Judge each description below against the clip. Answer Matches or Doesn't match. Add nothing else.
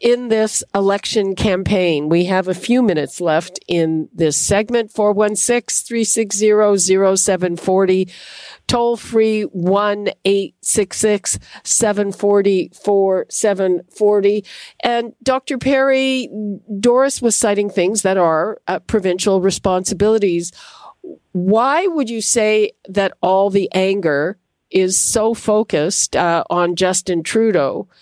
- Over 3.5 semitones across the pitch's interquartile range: Doesn't match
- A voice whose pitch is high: Matches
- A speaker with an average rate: Doesn't match